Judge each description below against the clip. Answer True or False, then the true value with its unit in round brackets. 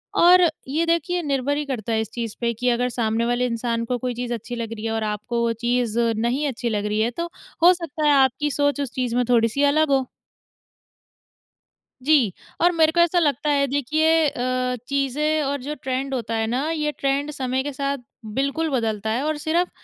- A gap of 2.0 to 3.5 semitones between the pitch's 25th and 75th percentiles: False (4.0 semitones)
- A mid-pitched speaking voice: False (265 Hz)